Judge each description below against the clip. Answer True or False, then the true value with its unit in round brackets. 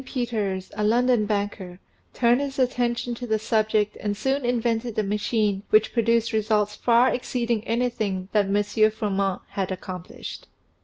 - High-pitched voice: True (220 Hz)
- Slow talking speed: False (145 wpm)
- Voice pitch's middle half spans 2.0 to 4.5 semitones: True (2.6 semitones)